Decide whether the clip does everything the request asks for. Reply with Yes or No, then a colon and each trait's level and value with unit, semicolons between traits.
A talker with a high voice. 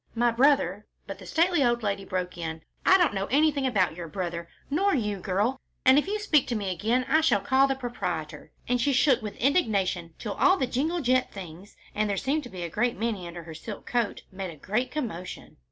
Yes: high, 225 Hz